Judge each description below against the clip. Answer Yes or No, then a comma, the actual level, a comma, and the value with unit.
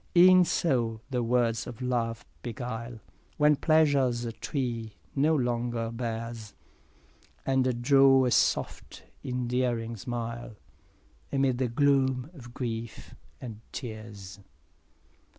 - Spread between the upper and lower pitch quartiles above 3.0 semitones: No, narrow, 2.5 semitones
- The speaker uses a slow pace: Yes, slow, 105 wpm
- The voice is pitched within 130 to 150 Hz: No, low, 120 Hz